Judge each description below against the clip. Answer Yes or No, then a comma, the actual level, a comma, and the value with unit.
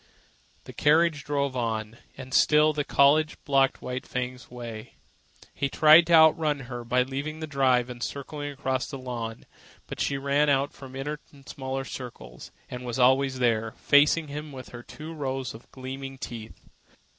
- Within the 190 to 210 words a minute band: No, average, 165 wpm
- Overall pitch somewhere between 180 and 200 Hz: No, low, 135 Hz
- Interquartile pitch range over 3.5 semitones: No, average, 2.7 semitones